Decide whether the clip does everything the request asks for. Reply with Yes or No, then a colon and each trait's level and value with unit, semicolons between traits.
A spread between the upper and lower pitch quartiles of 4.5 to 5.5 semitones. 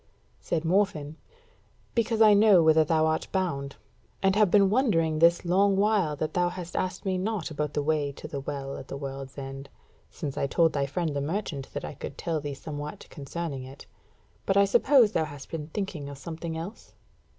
Yes: average, 5.1 semitones